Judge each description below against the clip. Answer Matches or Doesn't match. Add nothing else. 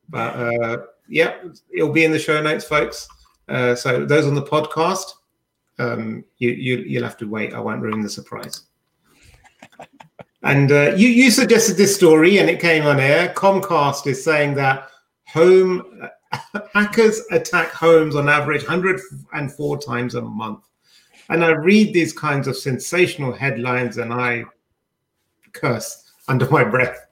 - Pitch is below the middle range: Doesn't match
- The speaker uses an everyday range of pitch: Doesn't match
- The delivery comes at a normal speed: Matches